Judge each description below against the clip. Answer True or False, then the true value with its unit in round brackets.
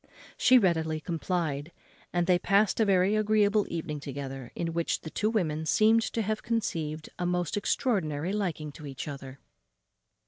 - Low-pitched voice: False (175 Hz)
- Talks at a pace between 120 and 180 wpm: True (160 wpm)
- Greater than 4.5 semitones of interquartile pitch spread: True (5.2 semitones)